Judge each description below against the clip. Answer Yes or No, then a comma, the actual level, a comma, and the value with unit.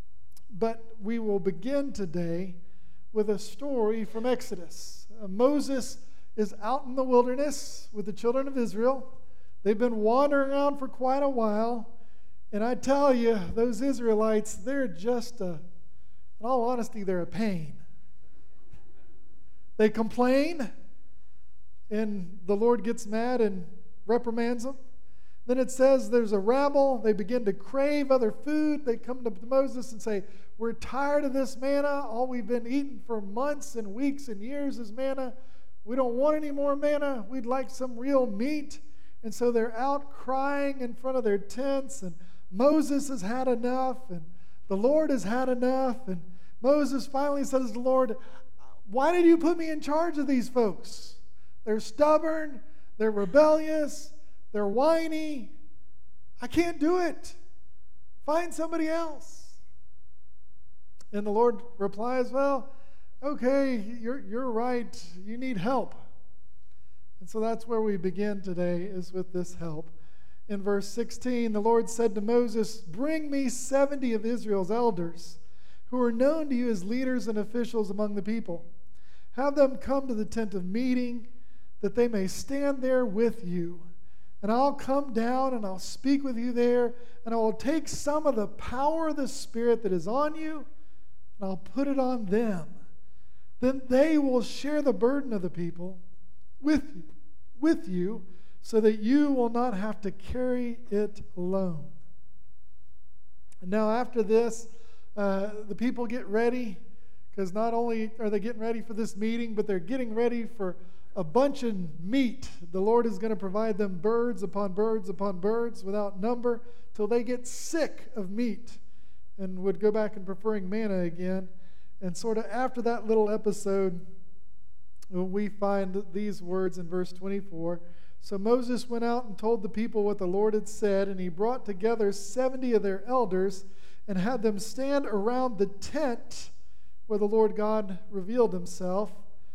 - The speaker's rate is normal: Yes, average, 160 wpm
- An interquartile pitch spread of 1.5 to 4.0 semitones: No, average, 4.4 semitones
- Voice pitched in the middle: No, high, 230 Hz